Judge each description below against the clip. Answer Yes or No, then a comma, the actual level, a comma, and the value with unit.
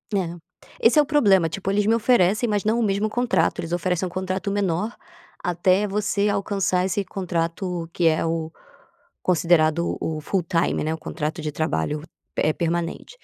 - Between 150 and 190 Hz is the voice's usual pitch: Yes, medium, 185 Hz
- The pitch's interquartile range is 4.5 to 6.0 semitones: No, average, 3.5 semitones